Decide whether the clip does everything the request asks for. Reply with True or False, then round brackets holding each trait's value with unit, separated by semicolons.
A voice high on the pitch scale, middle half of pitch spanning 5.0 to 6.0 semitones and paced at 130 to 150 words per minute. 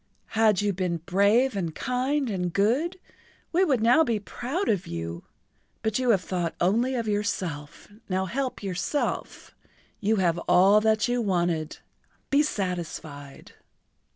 True (205 Hz; 5.5 semitones; 135 wpm)